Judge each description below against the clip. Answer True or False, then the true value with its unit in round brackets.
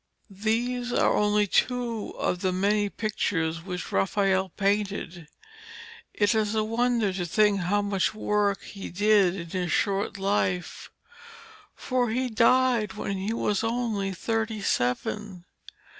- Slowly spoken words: True (130 wpm)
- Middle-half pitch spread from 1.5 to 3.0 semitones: True (2.6 semitones)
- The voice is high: True (205 Hz)